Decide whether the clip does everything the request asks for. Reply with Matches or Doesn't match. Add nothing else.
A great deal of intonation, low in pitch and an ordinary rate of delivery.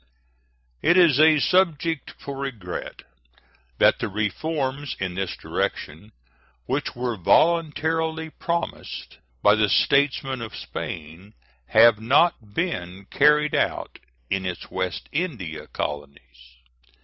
Doesn't match